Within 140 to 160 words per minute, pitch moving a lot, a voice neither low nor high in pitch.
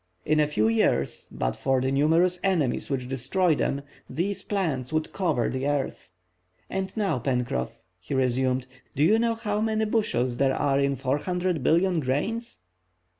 Yes: average, 155 wpm; wide, 6.3 semitones; medium, 145 Hz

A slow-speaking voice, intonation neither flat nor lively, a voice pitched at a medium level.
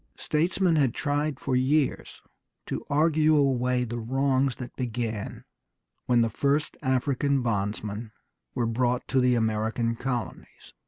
No: slow, 125 wpm; average, 3.4 semitones; low, 125 Hz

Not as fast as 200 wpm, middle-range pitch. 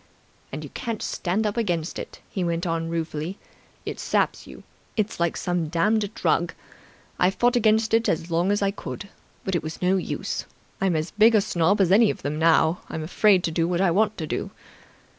No: fast, 205 wpm; medium, 180 Hz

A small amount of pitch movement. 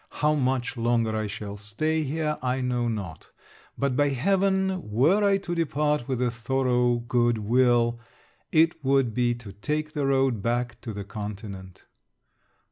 No: average, 4.6 semitones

